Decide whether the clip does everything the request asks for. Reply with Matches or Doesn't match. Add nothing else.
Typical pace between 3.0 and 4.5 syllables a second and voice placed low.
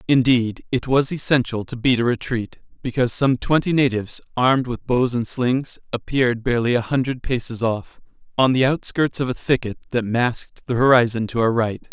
Doesn't match